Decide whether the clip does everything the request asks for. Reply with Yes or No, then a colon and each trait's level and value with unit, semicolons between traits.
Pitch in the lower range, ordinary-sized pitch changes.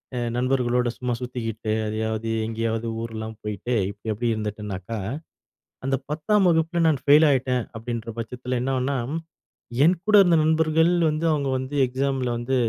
Yes: low, 125 Hz; average, 4.2 semitones